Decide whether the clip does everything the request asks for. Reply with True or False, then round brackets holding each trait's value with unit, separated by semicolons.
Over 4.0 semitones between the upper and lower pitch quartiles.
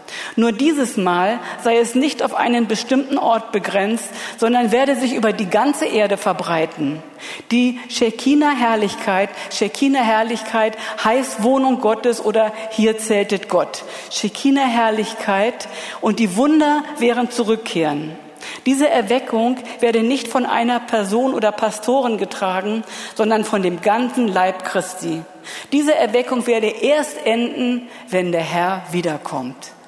False (3.2 semitones)